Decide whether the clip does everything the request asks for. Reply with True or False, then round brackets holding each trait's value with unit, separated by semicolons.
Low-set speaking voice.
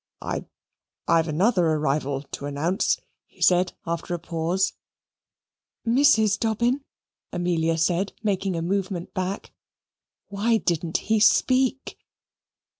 False (180 Hz)